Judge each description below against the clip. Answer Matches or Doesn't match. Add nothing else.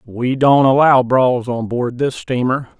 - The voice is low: Matches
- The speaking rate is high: Doesn't match